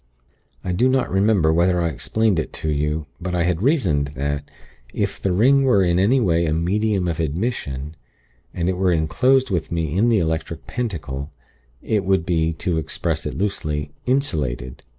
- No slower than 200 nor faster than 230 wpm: No, average, 175 wpm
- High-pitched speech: No, very low, 85 Hz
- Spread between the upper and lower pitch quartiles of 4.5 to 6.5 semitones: Yes, average, 4.8 semitones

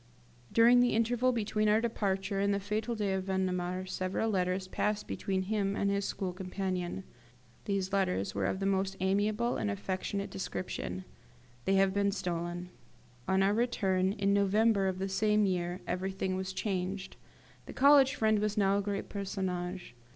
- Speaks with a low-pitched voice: No, high, 195 Hz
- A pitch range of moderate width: No, narrow, 1.9 semitones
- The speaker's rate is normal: Yes, average, 165 wpm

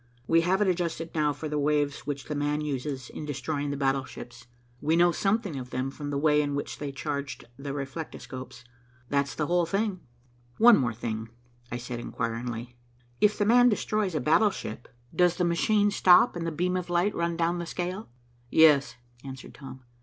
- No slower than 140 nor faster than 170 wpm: No, average, 185 wpm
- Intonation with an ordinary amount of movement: Yes, average, 4.4 semitones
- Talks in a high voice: No, medium, 150 Hz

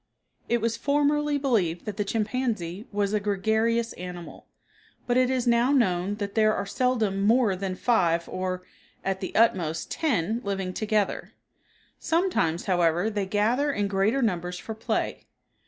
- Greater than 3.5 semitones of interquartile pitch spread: Yes, average, 4.1 semitones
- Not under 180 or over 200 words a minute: No, average, 150 wpm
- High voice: Yes, high, 210 Hz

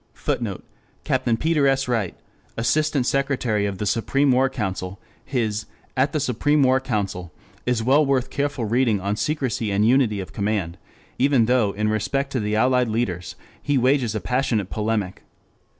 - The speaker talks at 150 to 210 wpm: Yes, average, 155 wpm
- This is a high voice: No, low, 120 Hz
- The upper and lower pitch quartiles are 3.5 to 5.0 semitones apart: Yes, average, 4.3 semitones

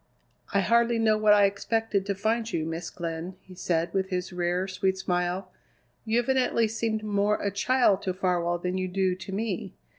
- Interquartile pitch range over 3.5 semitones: No, average, 3.2 semitones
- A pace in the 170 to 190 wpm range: Yes, average, 185 wpm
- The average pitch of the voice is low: No, high, 195 Hz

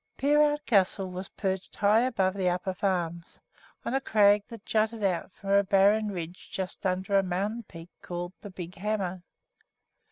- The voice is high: Yes, high, 195 Hz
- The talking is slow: No, average, 165 wpm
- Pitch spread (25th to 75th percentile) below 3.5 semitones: Yes, average, 2.7 semitones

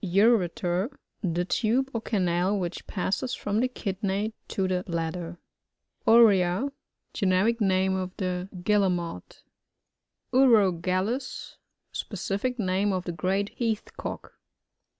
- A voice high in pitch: Yes, high, 195 Hz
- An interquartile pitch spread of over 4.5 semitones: No, average, 3.4 semitones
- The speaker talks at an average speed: No, slow, 115 wpm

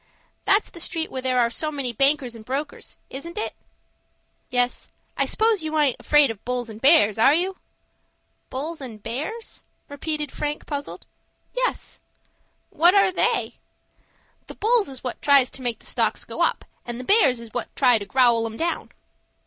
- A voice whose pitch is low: No, very high, 275 Hz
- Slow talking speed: No, average, 165 wpm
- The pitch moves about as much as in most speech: Yes, average, 4.8 semitones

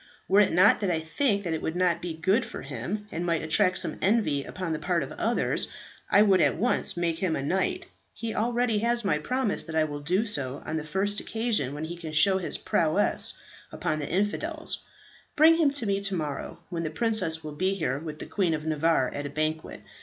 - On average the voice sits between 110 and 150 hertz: No, medium, 180 Hz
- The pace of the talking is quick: Yes, fast, 225 wpm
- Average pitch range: Yes, average, 4.9 semitones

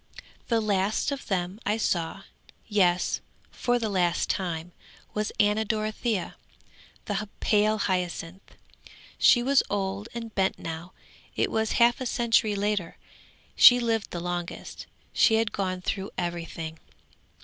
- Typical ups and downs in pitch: Yes, average, 3.6 semitones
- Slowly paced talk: Yes, slow, 130 wpm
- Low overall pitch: No, high, 205 Hz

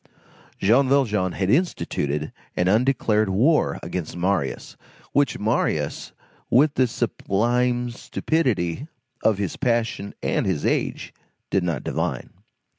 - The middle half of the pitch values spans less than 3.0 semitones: No, average, 5.2 semitones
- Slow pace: Yes, slow, 115 wpm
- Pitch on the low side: Yes, low, 110 Hz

